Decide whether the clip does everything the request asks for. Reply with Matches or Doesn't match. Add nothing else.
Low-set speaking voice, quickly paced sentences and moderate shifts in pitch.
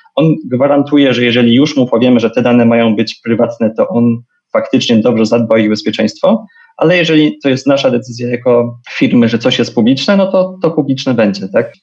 Matches